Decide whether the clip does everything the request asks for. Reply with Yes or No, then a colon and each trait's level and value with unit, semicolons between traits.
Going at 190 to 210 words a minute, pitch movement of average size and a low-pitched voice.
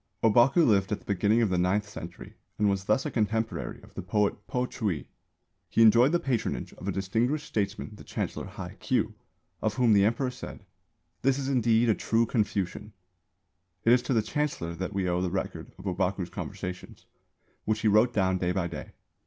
Yes: average, 195 wpm; average, 3.5 semitones; low, 105 Hz